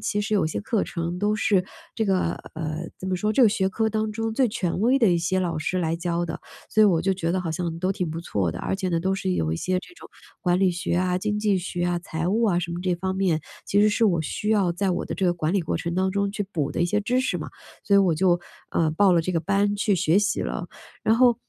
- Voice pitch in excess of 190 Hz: No, medium, 185 Hz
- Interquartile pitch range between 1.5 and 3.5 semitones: Yes, average, 3.2 semitones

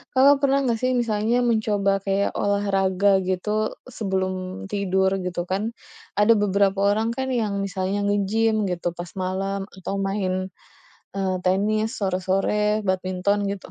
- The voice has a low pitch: No, high, 200 Hz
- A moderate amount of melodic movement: No, narrow, 2.0 semitones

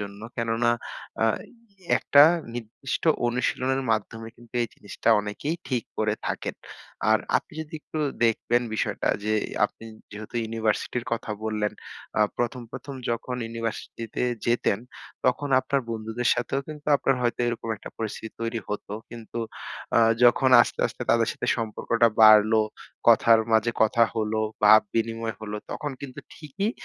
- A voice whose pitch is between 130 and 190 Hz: No, low, 115 Hz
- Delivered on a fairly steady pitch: Yes, narrow, 2.1 semitones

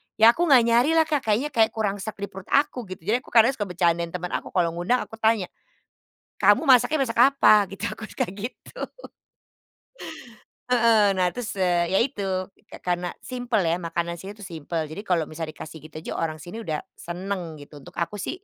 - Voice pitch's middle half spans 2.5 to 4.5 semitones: No, average, 5.1 semitones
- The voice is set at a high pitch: Yes, high, 195 Hz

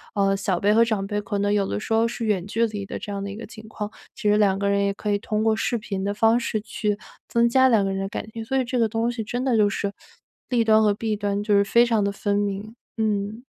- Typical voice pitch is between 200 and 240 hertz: Yes, high, 210 Hz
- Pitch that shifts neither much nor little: No, narrow, 2.0 semitones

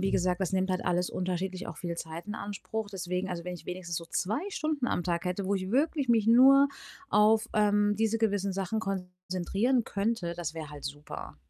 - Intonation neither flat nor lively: Yes, average, 3.6 semitones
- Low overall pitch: No, high, 190 Hz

